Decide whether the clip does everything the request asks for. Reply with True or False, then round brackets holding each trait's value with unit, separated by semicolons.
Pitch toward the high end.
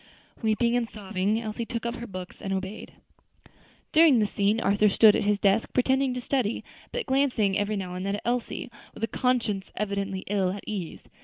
True (215 Hz)